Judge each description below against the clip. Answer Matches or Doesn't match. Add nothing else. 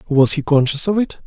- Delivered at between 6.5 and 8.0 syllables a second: Doesn't match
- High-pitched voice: Doesn't match